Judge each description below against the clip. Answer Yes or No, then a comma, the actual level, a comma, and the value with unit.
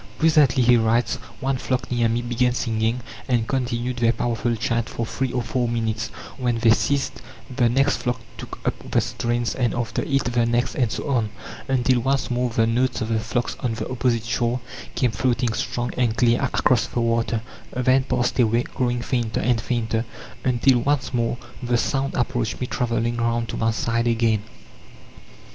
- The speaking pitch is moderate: No, low, 120 Hz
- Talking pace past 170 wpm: Yes, average, 180 wpm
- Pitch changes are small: Yes, narrow, 1.5 semitones